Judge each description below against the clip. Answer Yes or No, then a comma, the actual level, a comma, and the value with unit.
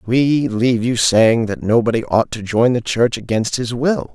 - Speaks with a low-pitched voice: Yes, low, 120 Hz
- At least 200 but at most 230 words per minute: Yes, fast, 205 wpm